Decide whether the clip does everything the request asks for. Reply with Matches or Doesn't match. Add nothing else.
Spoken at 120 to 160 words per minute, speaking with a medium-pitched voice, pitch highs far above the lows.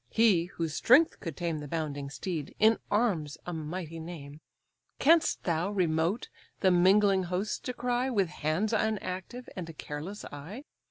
Doesn't match